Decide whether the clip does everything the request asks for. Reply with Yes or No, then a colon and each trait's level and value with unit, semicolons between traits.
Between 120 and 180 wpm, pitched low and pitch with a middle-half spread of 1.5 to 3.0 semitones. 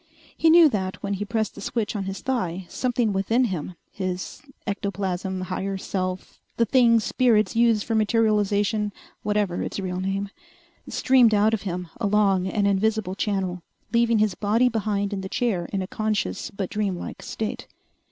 No: average, 165 wpm; high, 205 Hz; narrow, 2.6 semitones